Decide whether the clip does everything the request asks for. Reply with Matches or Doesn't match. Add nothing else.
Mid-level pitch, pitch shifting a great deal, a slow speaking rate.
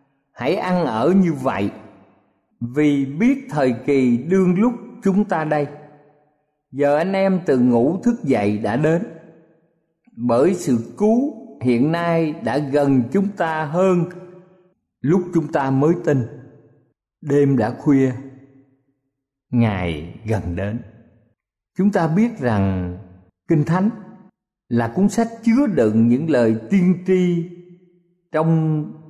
Matches